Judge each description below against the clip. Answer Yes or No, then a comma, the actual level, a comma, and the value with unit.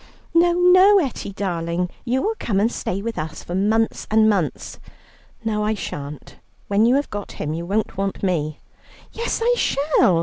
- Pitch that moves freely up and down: Yes, wide, 6.8 semitones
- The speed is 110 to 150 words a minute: No, average, 175 wpm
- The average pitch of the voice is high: Yes, high, 210 Hz